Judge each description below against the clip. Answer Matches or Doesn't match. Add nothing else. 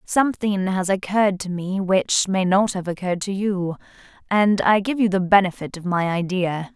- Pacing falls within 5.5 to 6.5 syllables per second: Doesn't match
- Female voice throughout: Matches